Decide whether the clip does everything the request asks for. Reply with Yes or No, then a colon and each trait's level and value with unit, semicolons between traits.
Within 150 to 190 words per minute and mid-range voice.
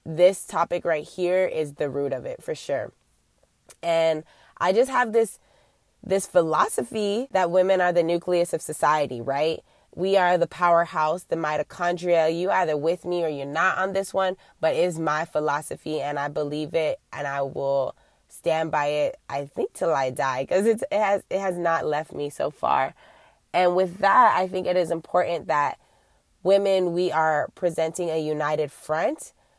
Yes: average, 175 wpm; medium, 170 Hz